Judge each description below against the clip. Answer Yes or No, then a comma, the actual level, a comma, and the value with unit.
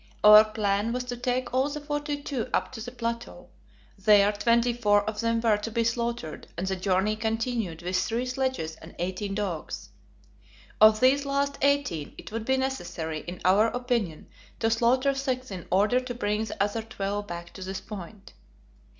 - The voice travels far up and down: No, average, 4.0 semitones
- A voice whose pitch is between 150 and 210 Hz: No, high, 225 Hz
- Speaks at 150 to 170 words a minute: No, average, 180 wpm